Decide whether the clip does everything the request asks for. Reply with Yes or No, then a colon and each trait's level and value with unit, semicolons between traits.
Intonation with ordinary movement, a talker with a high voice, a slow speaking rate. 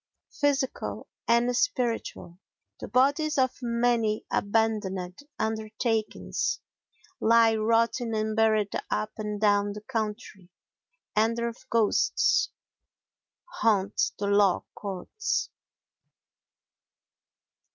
No: narrow, 2.1 semitones; high, 220 Hz; slow, 80 wpm